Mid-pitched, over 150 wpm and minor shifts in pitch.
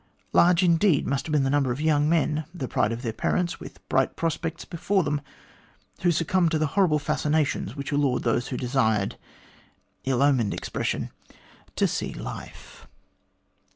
No: medium, 150 Hz; average, 160 wpm; average, 3.8 semitones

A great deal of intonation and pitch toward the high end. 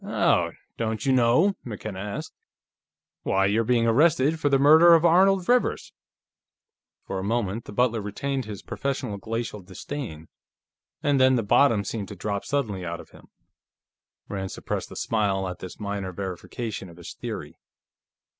No: wide, 5.7 semitones; low, 110 Hz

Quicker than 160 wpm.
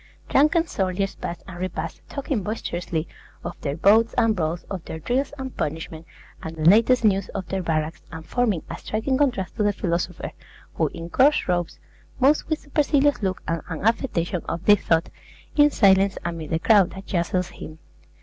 Yes: average, 180 wpm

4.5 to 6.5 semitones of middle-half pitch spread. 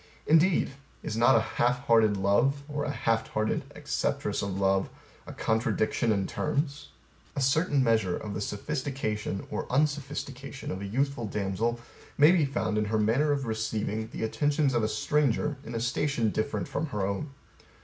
Yes: average, 4.9 semitones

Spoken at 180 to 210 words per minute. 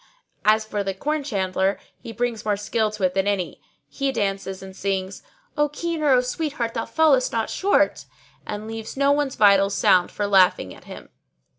Yes: average, 185 wpm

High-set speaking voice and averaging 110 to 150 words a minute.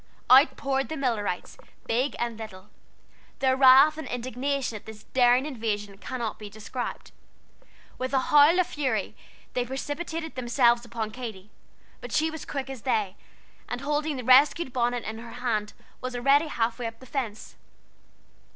No: very high, 250 Hz; average, 160 wpm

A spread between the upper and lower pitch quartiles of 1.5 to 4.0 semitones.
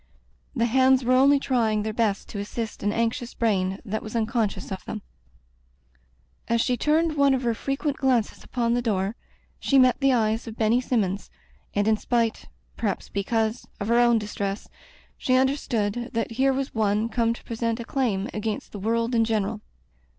Yes: average, 2.8 semitones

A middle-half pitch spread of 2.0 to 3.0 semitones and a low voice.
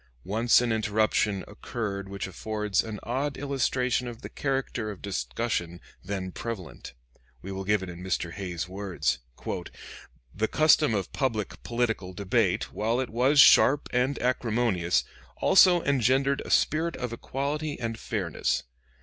No: average, 4.7 semitones; low, 110 Hz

